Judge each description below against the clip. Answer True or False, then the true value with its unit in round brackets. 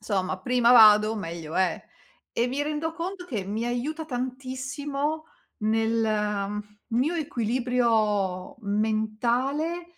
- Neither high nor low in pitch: False (235 Hz)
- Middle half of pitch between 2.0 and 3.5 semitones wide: False (4.7 semitones)